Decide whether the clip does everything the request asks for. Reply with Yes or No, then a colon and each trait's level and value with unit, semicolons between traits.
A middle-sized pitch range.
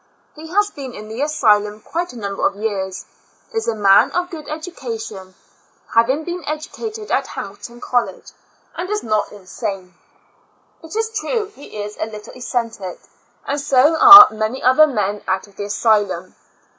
No: wide, 7.4 semitones